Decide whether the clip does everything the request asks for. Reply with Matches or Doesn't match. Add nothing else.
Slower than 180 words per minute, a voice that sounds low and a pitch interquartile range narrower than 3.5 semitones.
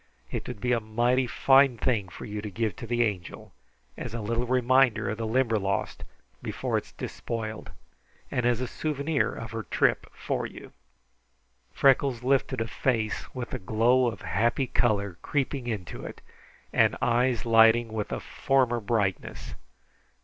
Matches